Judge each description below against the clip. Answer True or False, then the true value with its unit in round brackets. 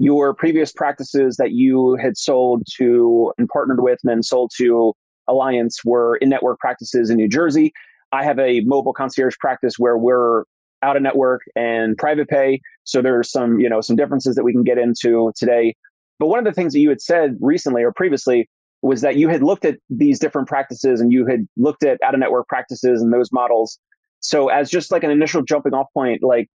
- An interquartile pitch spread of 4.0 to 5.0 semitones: False (3.2 semitones)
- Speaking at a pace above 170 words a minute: True (200 wpm)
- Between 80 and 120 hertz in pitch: False (130 Hz)